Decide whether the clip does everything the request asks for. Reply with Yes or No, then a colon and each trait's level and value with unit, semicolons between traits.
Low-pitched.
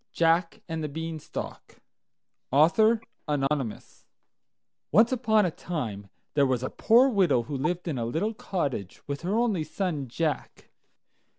No: medium, 160 Hz